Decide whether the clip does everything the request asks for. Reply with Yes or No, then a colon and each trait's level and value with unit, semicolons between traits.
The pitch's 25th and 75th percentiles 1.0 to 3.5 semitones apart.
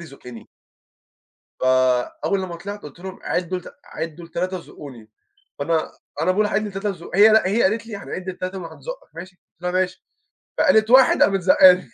Yes: average, 3.2 semitones